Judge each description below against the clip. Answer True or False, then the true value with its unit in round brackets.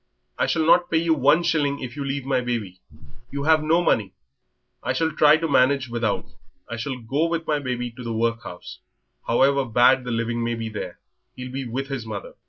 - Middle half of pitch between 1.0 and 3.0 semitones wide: False (4.1 semitones)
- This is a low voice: True (130 Hz)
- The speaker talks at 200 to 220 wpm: True (205 wpm)